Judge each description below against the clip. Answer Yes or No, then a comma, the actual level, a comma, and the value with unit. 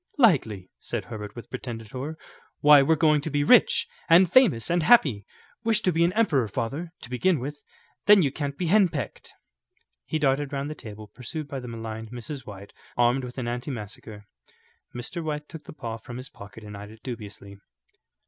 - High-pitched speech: No, low, 135 Hz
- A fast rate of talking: No, average, 185 wpm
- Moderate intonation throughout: No, wide, 5.8 semitones